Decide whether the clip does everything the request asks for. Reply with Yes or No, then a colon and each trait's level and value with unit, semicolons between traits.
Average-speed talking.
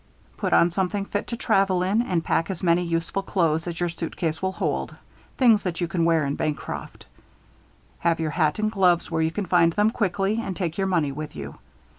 No: fast, 210 wpm